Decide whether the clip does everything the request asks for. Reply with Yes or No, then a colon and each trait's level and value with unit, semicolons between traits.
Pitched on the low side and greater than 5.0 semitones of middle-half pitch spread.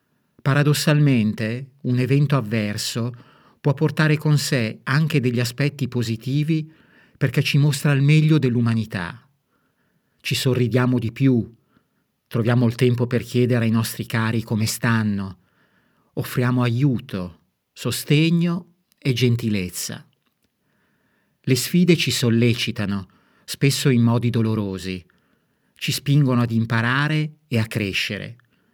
No: low, 125 Hz; average, 4.3 semitones